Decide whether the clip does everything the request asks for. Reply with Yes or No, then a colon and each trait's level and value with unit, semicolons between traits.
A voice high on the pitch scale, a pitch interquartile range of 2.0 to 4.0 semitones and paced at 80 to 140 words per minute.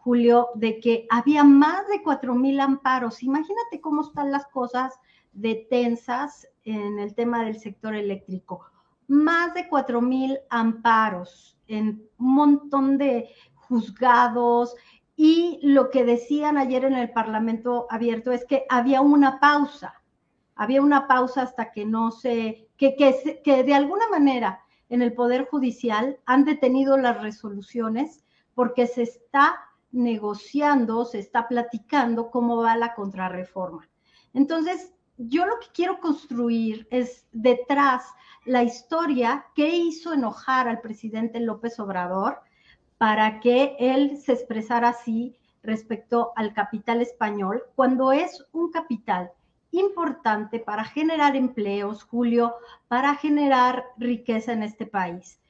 Yes: high, 245 Hz; average, 3.5 semitones; average, 130 wpm